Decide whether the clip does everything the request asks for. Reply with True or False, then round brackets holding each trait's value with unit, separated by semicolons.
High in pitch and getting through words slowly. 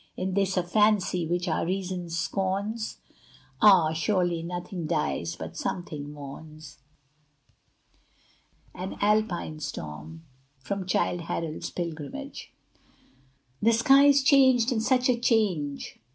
False (180 Hz; 110 wpm)